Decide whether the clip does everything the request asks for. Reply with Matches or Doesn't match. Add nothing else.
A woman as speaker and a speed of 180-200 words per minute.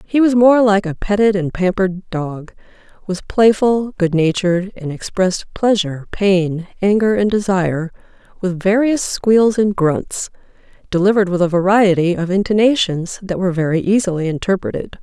Doesn't match